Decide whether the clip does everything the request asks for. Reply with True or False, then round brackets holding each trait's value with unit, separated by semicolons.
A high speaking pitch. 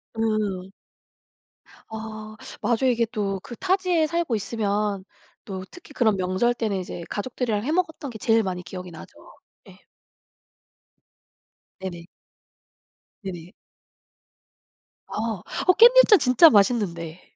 True (220 Hz)